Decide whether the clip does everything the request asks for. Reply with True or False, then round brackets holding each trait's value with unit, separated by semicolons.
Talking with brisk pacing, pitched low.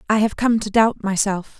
False (225 wpm; 210 Hz)